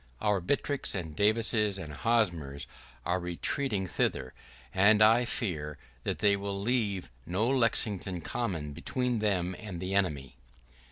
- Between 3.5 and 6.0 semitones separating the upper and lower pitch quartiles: Yes, average, 4.2 semitones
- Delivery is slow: Yes, slow, 130 wpm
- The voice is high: No, low, 100 Hz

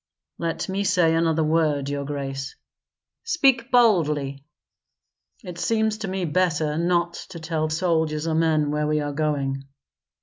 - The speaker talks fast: No, average, 140 wpm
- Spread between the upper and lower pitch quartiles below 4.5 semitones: Yes, average, 3.3 semitones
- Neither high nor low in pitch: Yes, medium, 160 Hz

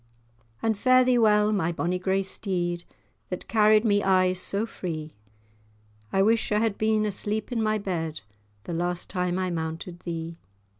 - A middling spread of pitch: Yes, average, 3.5 semitones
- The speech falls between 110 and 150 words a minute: No, average, 160 wpm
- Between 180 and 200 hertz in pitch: Yes, high, 190 Hz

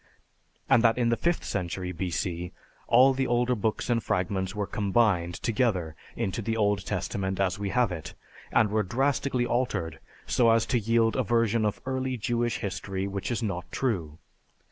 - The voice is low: Yes, low, 110 Hz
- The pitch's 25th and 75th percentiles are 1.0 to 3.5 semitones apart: No, average, 3.9 semitones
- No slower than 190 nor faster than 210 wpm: No, average, 170 wpm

